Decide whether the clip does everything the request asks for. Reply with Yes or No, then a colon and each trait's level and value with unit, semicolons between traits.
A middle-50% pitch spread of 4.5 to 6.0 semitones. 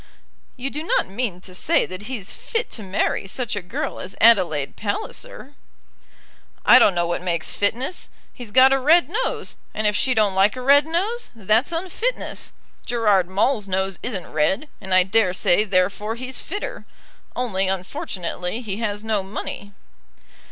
Yes: wide, 5.5 semitones